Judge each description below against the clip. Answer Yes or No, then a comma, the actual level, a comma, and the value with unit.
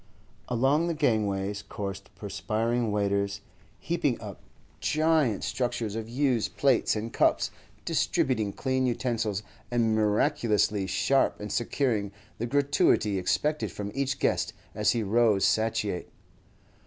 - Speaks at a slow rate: Yes, slow, 115 wpm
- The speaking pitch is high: No, low, 115 Hz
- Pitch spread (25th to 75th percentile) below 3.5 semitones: No, average, 4.2 semitones